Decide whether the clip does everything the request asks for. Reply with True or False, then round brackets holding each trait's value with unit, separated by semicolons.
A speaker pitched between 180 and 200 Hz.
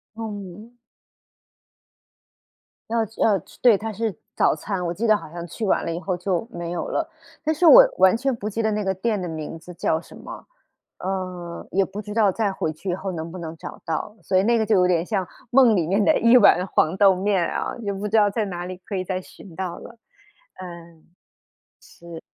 True (190 Hz)